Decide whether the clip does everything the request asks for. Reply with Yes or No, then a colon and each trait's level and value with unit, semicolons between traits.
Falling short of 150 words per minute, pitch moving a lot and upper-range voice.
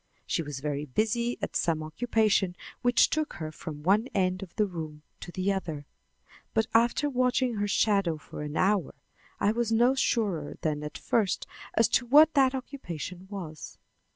No: average, 165 wpm; wide, 6.7 semitones; high, 200 Hz